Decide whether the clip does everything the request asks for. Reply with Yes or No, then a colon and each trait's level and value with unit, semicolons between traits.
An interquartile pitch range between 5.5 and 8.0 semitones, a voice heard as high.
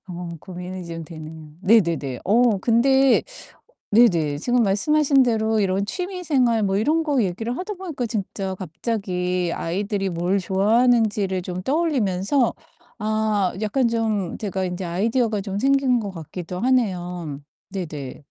No: average, 5.1 semitones; high, 205 Hz